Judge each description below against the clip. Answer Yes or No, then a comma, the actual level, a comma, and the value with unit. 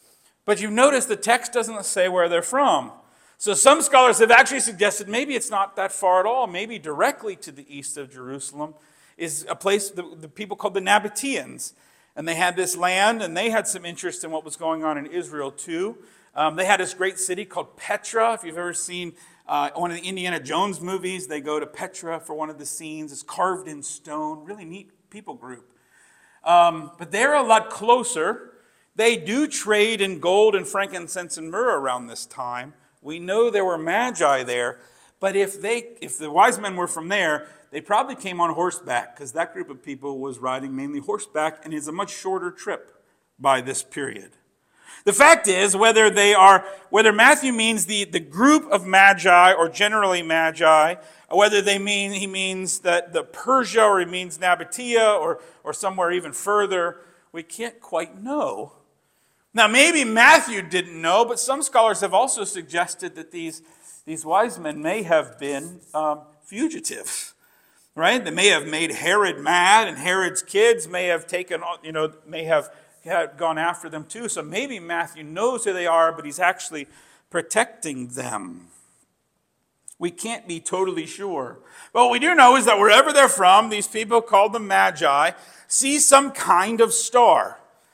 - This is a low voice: No, medium, 185 Hz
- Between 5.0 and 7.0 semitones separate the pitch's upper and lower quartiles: Yes, average, 5.3 semitones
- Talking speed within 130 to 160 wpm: No, average, 185 wpm